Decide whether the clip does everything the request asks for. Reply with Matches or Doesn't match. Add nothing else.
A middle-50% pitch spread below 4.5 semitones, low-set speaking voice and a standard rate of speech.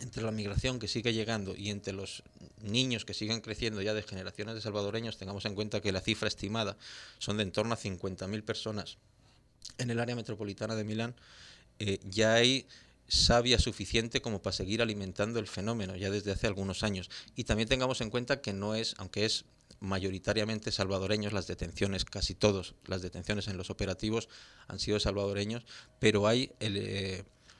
Matches